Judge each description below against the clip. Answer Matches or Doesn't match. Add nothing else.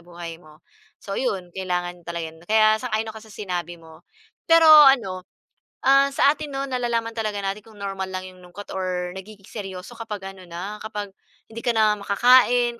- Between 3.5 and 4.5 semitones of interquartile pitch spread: Matches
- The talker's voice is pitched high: Matches